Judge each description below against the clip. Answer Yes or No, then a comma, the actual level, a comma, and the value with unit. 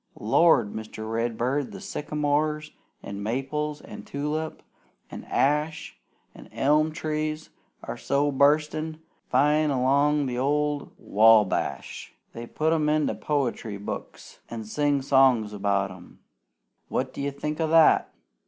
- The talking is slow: Yes, slow, 125 wpm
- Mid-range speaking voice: Yes, medium, 145 Hz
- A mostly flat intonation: No, average, 4.5 semitones